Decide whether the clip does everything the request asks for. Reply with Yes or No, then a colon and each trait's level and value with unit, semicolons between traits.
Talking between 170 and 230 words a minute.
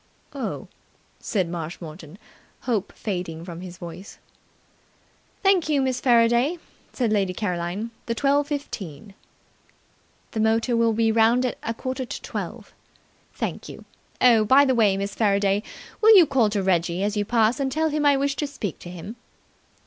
No: average, 160 wpm